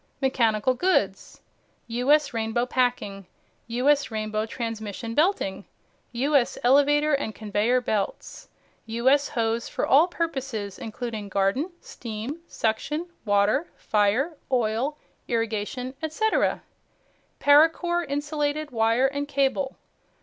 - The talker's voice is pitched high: Yes, very high, 250 Hz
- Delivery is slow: Yes, slow, 100 wpm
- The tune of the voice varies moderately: Yes, average, 4.8 semitones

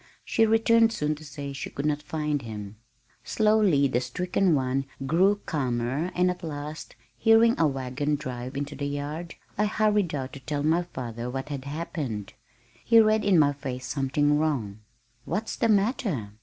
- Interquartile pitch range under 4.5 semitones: No, average, 5.3 semitones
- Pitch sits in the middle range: Yes, medium, 150 Hz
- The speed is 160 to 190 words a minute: Yes, average, 170 wpm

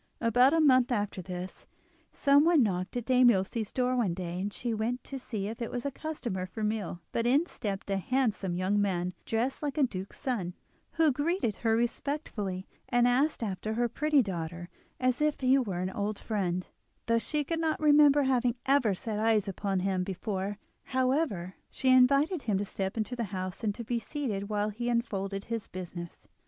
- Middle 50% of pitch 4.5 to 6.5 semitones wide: Yes, average, 5.0 semitones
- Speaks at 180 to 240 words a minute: Yes, average, 190 wpm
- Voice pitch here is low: No, high, 225 Hz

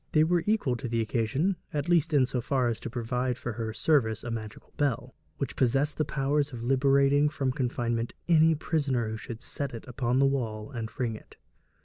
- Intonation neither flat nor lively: Yes, average, 3.6 semitones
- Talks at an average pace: No, fast, 210 wpm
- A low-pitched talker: Yes, low, 130 Hz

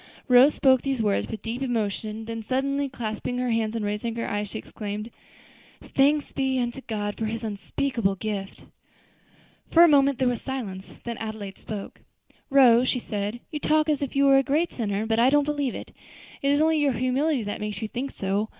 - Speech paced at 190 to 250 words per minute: Yes, average, 200 wpm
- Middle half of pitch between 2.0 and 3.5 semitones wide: No, average, 4.2 semitones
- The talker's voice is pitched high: Yes, high, 240 Hz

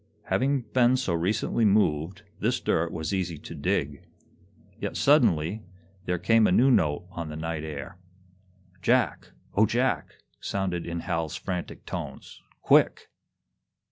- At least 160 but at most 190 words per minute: No, slow, 135 wpm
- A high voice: No, very low, 90 Hz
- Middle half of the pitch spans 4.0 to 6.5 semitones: Yes, average, 5.1 semitones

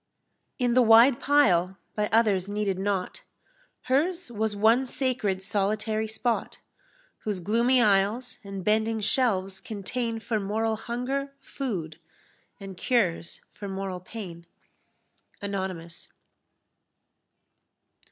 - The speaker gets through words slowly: Yes, slow, 105 wpm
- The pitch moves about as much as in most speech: Yes, average, 3.6 semitones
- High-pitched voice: Yes, high, 215 Hz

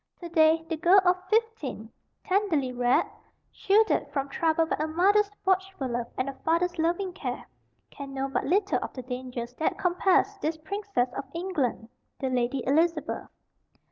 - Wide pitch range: Yes, wide, 6.0 semitones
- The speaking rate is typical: Yes, average, 160 wpm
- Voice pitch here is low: No, very high, 325 Hz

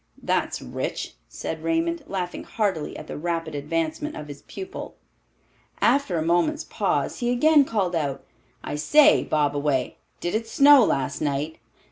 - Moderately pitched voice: Yes, medium, 175 Hz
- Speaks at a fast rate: No, average, 145 wpm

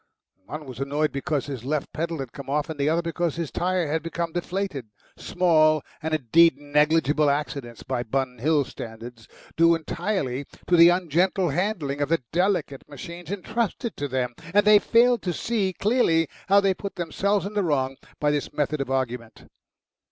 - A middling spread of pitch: Yes, average, 4.4 semitones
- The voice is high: No, medium, 155 Hz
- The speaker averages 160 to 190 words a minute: Yes, average, 175 wpm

